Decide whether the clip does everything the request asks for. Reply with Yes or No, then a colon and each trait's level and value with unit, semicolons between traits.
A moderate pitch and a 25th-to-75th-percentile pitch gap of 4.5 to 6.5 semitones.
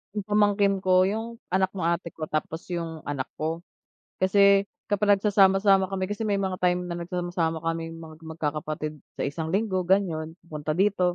No: medium, 180 Hz; average, 3.3 semitones